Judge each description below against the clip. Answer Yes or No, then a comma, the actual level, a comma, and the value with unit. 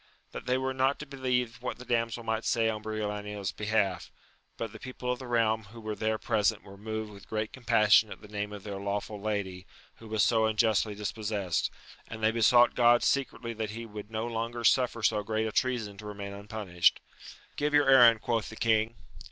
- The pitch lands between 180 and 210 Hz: No, low, 110 Hz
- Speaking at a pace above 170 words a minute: Yes, average, 200 wpm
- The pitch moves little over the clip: Yes, narrow, 2.1 semitones